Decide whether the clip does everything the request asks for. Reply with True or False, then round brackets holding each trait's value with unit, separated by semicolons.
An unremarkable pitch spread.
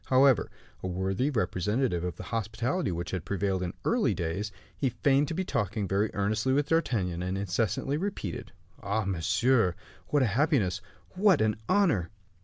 False (6.4 semitones)